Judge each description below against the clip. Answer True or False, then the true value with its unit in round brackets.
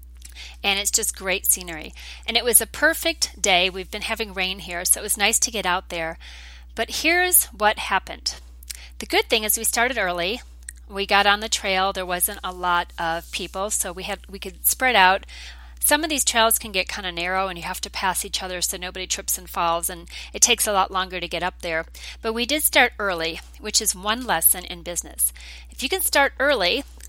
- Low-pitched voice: False (190 Hz)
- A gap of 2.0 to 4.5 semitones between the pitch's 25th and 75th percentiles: True (4.2 semitones)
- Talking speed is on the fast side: True (220 wpm)